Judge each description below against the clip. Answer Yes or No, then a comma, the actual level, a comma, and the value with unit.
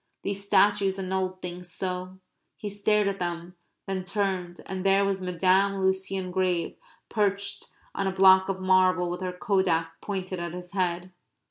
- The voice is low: No, high, 190 Hz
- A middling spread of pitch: No, narrow, 1.3 semitones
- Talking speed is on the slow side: No, average, 155 wpm